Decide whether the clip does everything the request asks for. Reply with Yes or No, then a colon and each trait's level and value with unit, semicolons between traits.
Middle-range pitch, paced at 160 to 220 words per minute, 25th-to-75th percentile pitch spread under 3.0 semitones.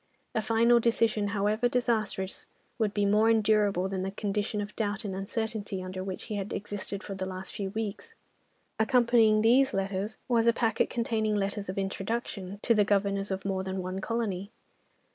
No: high, 205 Hz; average, 175 wpm; narrow, 2.5 semitones